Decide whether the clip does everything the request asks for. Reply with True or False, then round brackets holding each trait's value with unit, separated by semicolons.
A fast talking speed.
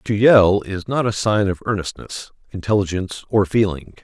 False (165 wpm)